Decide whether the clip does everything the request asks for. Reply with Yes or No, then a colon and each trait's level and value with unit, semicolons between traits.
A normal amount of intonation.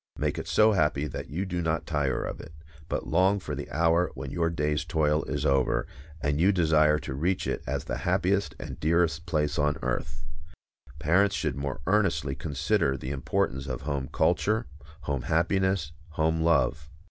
Yes: average, 3.4 semitones